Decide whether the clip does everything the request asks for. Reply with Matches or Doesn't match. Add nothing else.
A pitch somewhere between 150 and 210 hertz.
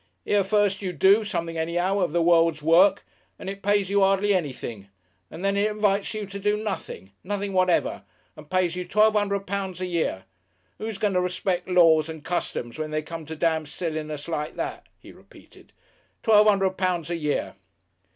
Matches